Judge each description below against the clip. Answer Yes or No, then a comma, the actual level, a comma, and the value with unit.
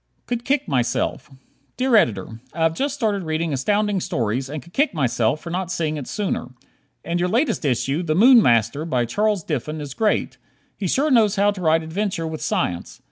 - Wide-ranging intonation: Yes, wide, 7.0 semitones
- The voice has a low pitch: No, medium, 165 Hz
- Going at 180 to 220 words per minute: Yes, average, 190 wpm